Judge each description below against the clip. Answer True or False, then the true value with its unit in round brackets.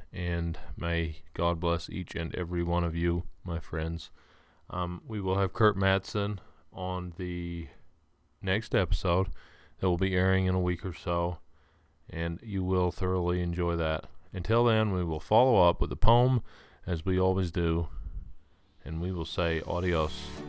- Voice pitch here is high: False (85 Hz)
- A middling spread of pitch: False (2.1 semitones)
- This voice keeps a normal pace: True (160 wpm)